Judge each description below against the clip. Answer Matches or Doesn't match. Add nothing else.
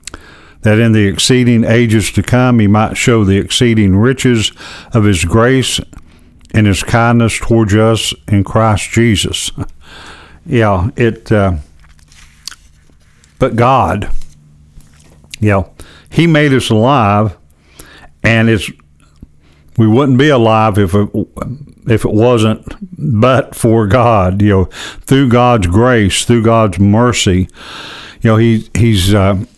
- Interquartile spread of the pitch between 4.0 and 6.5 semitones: Matches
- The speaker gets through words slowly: Matches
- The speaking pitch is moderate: Doesn't match